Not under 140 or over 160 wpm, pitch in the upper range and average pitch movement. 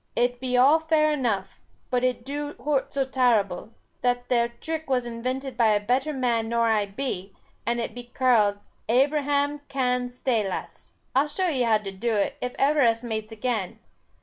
No: average, 175 wpm; high, 245 Hz; average, 3.2 semitones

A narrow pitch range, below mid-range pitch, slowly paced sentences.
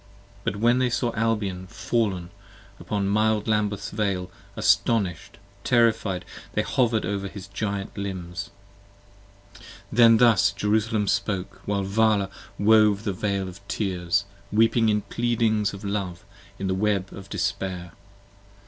Yes: narrow, 2.2 semitones; low, 100 Hz; slow, 130 wpm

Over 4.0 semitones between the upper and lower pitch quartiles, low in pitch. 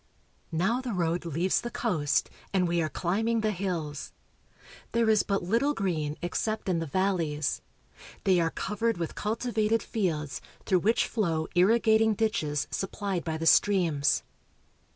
No: average, 5.0 semitones; medium, 185 Hz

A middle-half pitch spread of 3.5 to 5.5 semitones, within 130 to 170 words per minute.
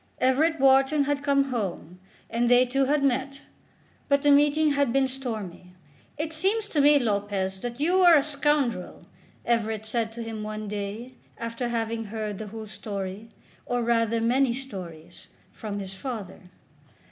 Yes: average, 4.6 semitones; average, 160 wpm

